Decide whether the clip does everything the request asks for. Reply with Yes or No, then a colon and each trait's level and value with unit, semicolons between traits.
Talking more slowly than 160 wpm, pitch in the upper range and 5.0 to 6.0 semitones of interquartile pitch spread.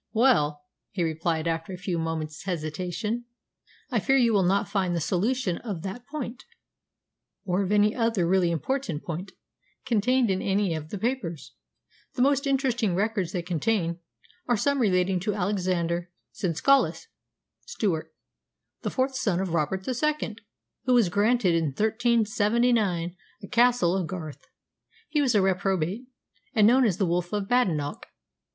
Yes: average, 150 wpm; high, 195 Hz; wide, 5.5 semitones